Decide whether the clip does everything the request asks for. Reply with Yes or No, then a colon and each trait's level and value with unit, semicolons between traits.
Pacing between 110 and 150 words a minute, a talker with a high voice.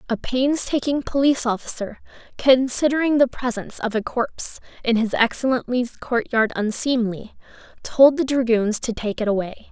Yes: slow, 135 wpm; high, 245 Hz